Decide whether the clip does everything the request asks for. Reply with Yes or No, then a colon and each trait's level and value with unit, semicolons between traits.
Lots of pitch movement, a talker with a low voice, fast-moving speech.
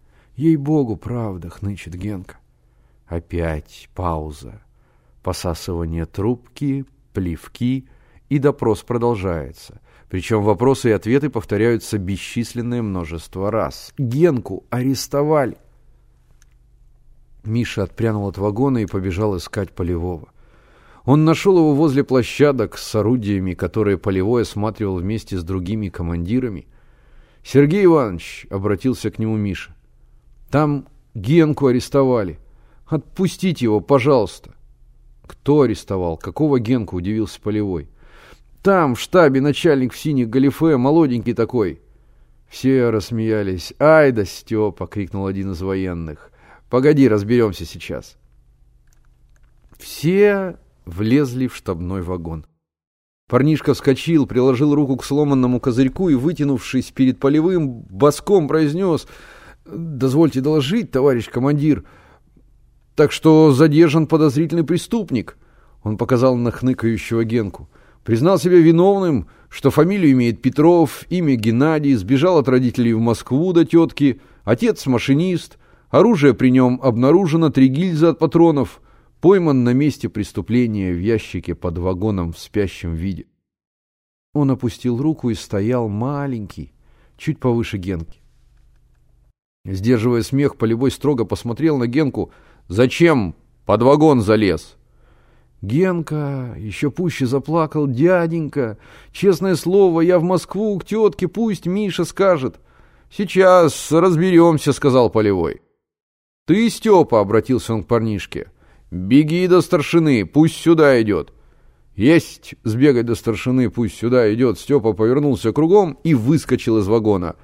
No: wide, 7.3 semitones; low, 120 Hz; slow, 110 wpm